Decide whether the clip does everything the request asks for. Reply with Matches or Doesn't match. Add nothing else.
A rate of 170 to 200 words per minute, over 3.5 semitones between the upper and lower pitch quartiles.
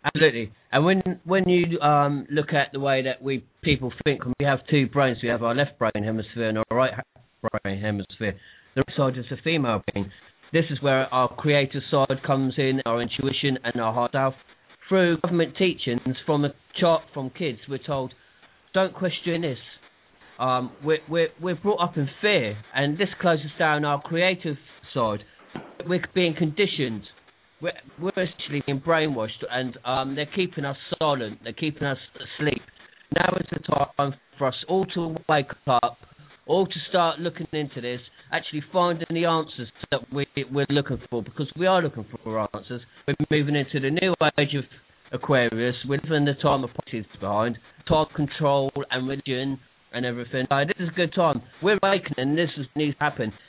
Matches